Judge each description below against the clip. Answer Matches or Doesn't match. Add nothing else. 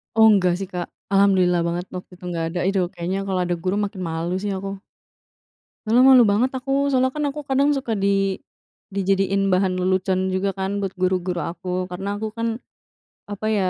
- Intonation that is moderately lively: Doesn't match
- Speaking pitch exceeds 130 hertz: Matches